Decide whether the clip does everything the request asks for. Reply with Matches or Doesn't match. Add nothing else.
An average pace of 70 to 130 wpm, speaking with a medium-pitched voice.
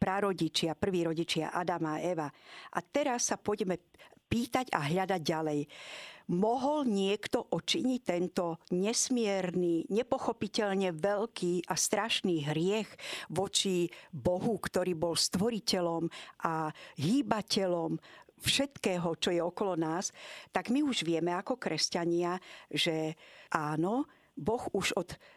Matches